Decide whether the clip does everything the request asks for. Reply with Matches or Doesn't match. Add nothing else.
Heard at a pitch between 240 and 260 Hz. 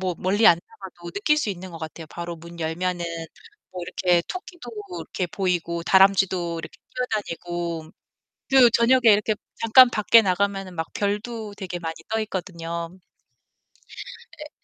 Doesn't match